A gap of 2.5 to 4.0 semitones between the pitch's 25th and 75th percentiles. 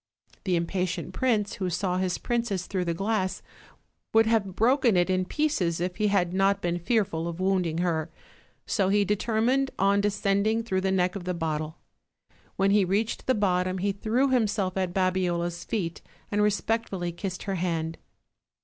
Yes: average, 2.8 semitones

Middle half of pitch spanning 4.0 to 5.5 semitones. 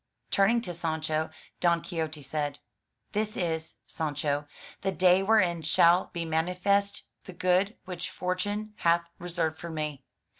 No: average, 2.9 semitones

